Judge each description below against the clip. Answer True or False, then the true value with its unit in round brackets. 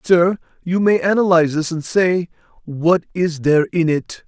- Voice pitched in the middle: True (170 Hz)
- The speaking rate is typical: True (170 wpm)